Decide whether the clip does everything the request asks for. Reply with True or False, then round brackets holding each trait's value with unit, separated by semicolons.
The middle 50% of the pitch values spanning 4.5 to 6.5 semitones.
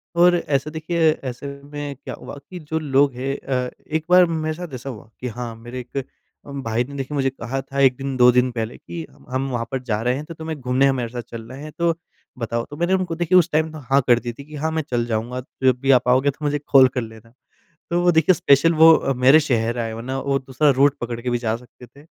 False (4.0 semitones)